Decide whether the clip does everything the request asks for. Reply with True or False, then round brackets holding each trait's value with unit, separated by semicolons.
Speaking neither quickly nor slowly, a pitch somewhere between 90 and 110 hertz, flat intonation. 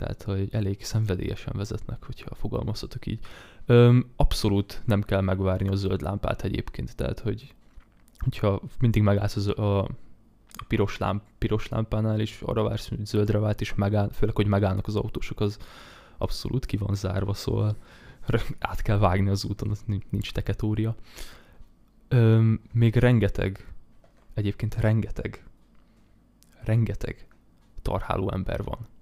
True (135 wpm; 105 Hz; 2.2 semitones)